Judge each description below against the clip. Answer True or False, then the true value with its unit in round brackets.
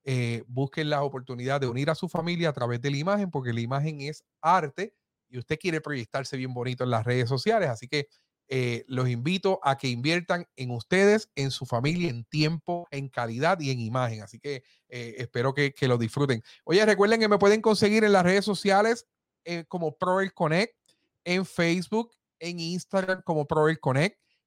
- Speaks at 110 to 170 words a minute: False (190 wpm)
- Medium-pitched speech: True (150 Hz)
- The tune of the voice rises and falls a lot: True (5.9 semitones)